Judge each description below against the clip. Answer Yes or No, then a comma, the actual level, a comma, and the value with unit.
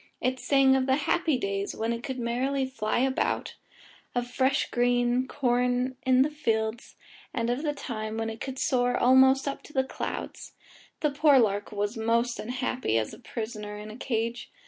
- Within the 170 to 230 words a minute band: Yes, average, 180 wpm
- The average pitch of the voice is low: No, high, 245 Hz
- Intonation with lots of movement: No, average, 2.8 semitones